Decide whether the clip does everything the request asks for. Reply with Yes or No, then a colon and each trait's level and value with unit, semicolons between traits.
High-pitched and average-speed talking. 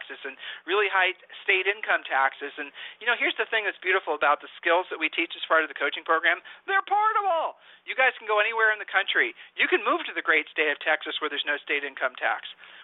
No: high, 210 Hz; fast, 235 wpm